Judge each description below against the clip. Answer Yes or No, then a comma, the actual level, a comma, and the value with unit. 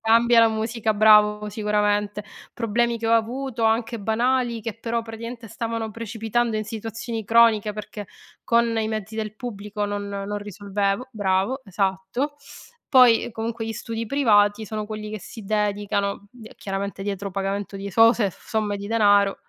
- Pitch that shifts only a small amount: Yes, narrow, 2.0 semitones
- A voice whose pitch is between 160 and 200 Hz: No, high, 215 Hz